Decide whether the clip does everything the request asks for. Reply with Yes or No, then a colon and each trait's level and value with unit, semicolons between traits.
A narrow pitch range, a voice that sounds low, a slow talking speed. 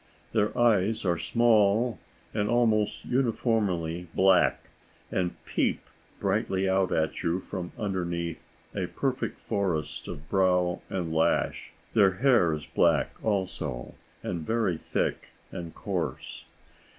No: average, 4.2 semitones; very low, 95 Hz; slow, 115 wpm